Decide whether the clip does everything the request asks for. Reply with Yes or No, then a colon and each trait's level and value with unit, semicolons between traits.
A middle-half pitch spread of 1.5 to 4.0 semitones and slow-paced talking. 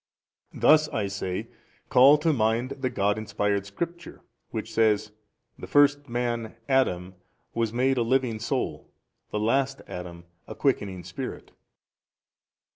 No: average, 4.7 semitones; slow, 130 wpm